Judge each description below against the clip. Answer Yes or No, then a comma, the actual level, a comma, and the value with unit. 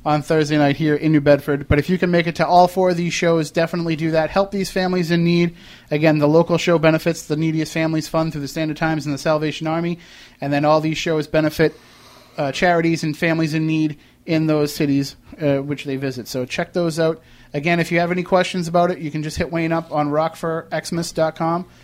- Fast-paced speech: Yes, fast, 230 wpm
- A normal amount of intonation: No, narrow, 2.1 semitones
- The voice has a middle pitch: Yes, medium, 160 Hz